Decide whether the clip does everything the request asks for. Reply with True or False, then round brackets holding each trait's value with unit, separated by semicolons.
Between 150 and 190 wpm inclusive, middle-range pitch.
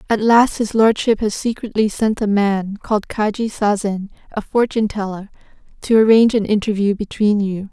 False (165 wpm; 210 Hz)